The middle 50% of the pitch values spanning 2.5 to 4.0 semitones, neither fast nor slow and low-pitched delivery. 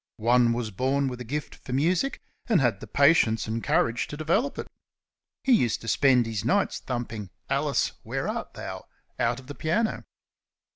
No: average, 5.0 semitones; average, 180 wpm; low, 125 Hz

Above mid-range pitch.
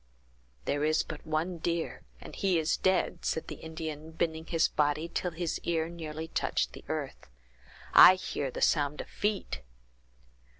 No: medium, 160 Hz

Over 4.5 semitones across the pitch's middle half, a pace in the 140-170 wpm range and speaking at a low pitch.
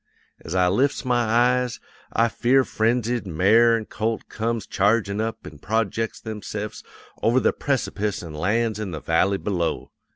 No: average, 3.1 semitones; average, 155 wpm; low, 110 Hz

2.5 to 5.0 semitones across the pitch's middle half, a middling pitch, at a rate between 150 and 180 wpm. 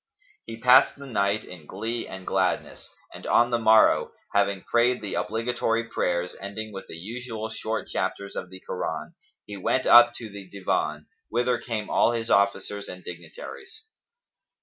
No: average, 3.6 semitones; low, 110 Hz; average, 160 wpm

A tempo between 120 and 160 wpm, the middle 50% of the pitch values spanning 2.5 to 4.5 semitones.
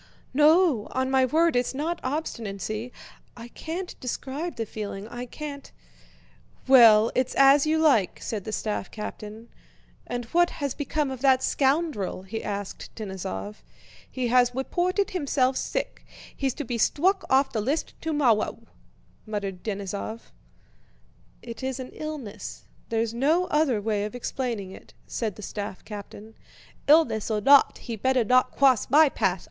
No: average, 145 wpm; average, 5.1 semitones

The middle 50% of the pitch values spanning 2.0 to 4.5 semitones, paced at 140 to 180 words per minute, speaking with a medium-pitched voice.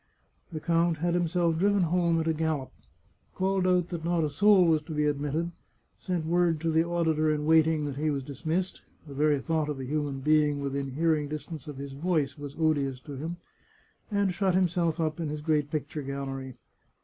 No: average, 2.7 semitones; average, 195 wpm; medium, 155 Hz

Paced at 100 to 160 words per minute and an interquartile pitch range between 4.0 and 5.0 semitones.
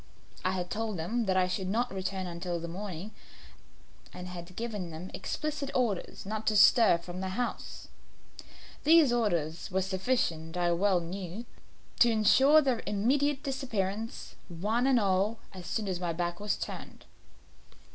Yes: average, 155 wpm; average, 4.5 semitones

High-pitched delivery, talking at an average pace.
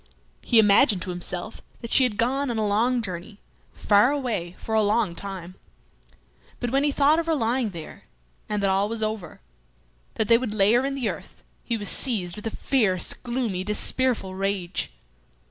Yes: high, 220 Hz; average, 180 wpm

